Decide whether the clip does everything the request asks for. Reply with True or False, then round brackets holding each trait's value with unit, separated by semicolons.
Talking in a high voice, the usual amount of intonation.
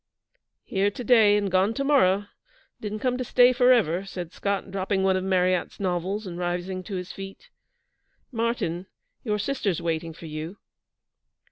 True (195 Hz; 3.3 semitones)